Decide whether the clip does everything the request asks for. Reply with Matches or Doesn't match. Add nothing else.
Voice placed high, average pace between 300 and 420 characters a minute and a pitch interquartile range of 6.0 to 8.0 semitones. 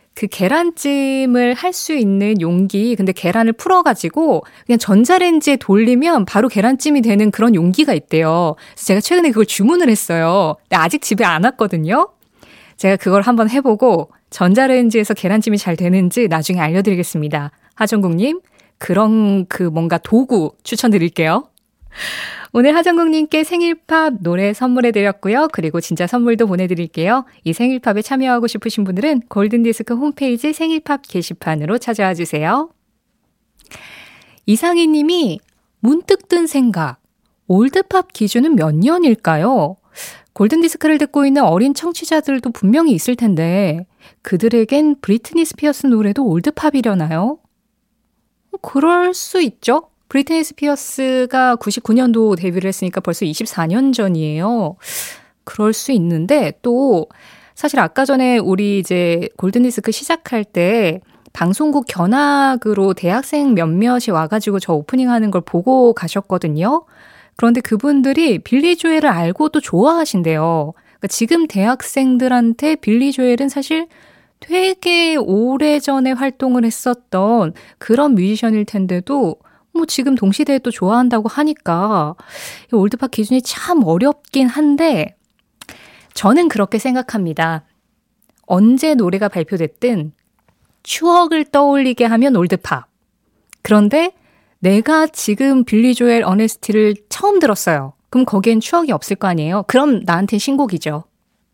Matches